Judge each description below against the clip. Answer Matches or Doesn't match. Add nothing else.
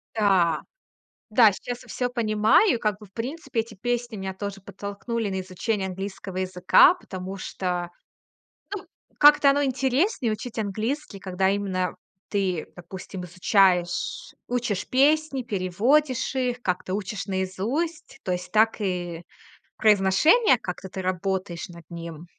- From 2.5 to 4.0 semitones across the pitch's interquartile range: Doesn't match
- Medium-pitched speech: Doesn't match